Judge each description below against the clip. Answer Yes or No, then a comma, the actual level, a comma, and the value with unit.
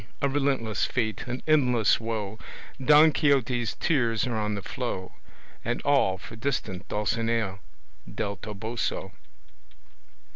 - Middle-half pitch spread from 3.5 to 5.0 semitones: Yes, average, 4.0 semitones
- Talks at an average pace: No, slow, 115 wpm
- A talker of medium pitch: No, low, 115 Hz